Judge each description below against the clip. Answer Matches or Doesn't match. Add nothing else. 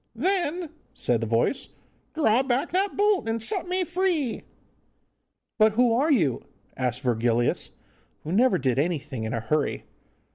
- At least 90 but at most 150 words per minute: Matches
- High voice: Matches